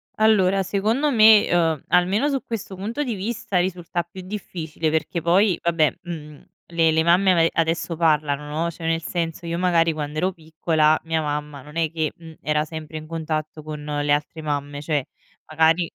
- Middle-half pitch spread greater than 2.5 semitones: Yes, average, 2.9 semitones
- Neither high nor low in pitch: Yes, medium, 165 Hz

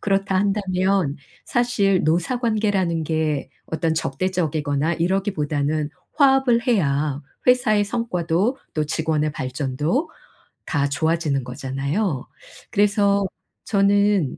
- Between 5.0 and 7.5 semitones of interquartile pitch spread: Yes, average, 5.3 semitones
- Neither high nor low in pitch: Yes, medium, 175 Hz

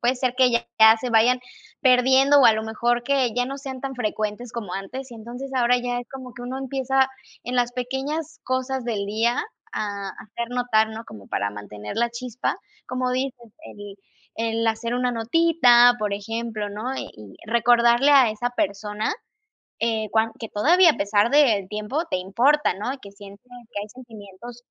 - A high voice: Yes, high, 240 Hz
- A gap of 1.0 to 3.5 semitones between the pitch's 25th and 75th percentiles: Yes, average, 3.1 semitones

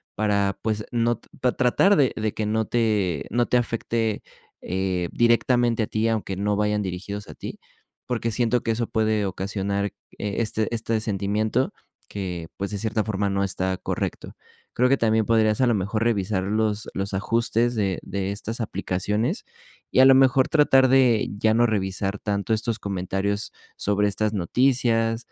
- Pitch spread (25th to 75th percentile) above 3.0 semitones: No, average, 2.7 semitones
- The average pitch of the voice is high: No, low, 110 Hz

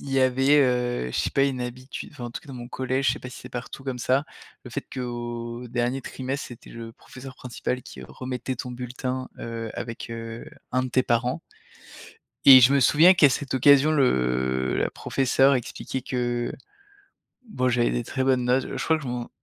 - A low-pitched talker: Yes, low, 125 Hz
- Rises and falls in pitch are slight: Yes, narrow, 1.7 semitones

